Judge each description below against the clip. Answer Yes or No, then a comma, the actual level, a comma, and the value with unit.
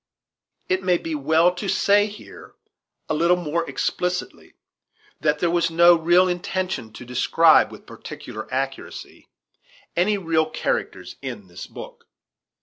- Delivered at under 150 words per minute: Yes, slow, 135 wpm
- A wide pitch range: No, average, 2.8 semitones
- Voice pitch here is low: No, medium, 175 Hz